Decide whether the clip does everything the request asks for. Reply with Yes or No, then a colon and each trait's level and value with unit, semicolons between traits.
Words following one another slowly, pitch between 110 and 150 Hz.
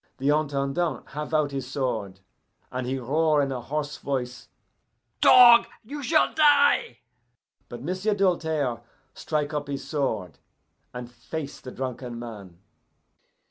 Yes: slow, 130 wpm; medium, 140 Hz